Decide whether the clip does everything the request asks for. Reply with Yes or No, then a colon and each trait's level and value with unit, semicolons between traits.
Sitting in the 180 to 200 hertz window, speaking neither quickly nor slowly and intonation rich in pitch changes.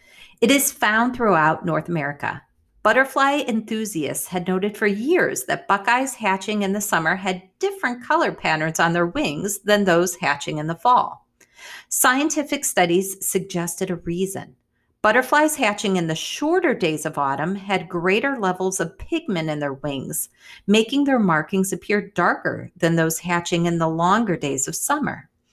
Yes: high, 190 Hz; average, 155 wpm; wide, 5.8 semitones